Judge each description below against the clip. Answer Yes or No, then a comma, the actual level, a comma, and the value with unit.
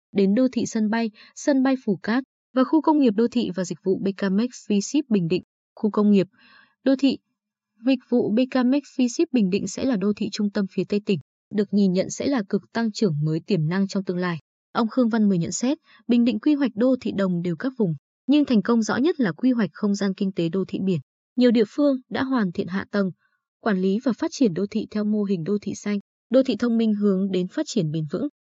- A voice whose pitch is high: Yes, high, 215 Hz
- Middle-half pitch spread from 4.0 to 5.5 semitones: Yes, average, 4.4 semitones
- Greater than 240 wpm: Yes, fast, 250 wpm